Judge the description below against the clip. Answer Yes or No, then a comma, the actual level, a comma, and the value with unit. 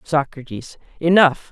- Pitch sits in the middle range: Yes, medium, 155 Hz